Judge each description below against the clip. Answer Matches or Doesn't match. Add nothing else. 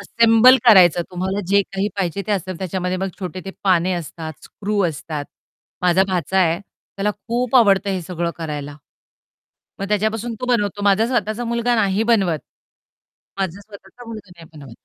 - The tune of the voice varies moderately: Matches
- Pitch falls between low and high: Doesn't match